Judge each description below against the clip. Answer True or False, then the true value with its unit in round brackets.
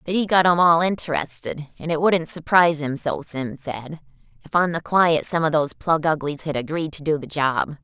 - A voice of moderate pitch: True (155 Hz)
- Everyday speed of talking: False (220 wpm)